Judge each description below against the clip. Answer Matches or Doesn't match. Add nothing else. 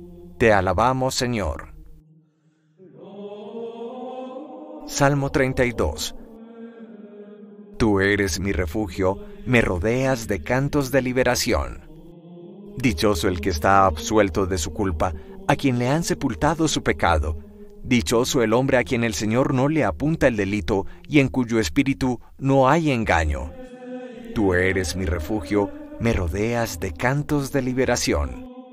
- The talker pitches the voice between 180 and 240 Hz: Doesn't match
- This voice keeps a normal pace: Doesn't match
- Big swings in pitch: Matches